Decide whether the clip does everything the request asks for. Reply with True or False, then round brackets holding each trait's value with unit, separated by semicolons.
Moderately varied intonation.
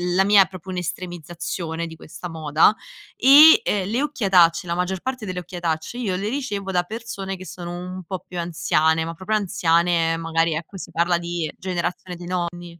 False (2.3 semitones)